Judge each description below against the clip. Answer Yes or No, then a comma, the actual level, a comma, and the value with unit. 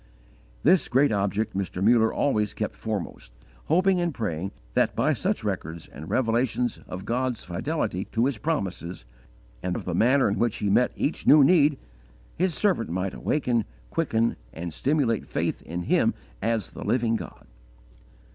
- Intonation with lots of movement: Yes, wide, 6.2 semitones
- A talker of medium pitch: No, low, 115 Hz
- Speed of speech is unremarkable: Yes, average, 160 wpm